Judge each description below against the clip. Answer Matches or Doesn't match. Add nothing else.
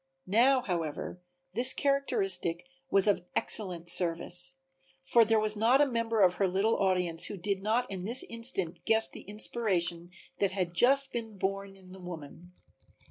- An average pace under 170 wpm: Matches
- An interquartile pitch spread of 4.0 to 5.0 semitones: Matches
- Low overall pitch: Doesn't match